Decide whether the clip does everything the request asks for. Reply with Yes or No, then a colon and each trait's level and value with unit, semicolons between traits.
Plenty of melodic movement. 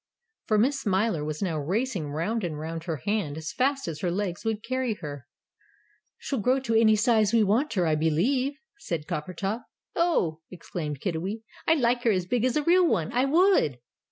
Yes: wide, 7.4 semitones